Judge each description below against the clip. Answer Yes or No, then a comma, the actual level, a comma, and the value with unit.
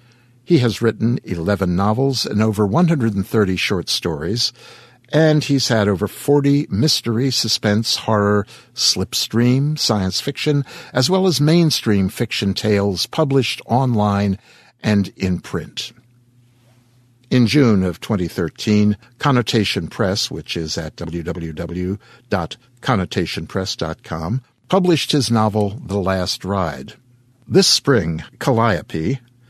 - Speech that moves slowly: Yes, slow, 105 wpm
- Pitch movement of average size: Yes, average, 4.2 semitones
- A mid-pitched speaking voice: No, low, 115 Hz